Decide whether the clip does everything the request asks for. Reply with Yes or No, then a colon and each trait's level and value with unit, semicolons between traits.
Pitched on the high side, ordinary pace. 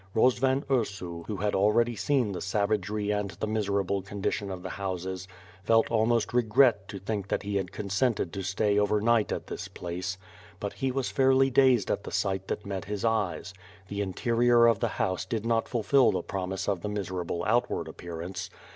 No: low, 105 Hz; average, 185 wpm